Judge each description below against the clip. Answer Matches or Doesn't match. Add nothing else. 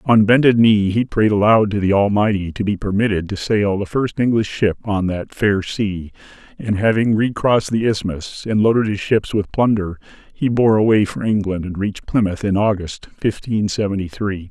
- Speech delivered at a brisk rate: Doesn't match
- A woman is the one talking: Doesn't match